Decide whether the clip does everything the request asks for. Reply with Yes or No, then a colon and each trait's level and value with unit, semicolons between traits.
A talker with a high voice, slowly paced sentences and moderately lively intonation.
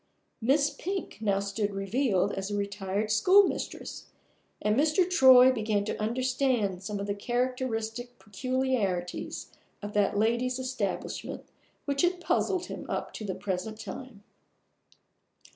Yes: high, 225 Hz; slow, 125 wpm; average, 4.3 semitones